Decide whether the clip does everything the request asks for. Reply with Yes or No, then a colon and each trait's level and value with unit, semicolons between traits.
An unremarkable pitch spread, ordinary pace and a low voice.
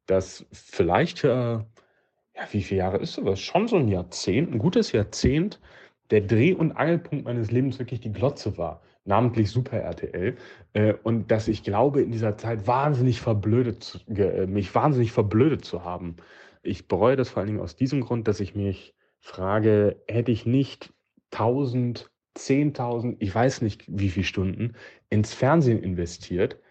Yes: average, 3.6 semitones; average, 160 wpm; low, 115 Hz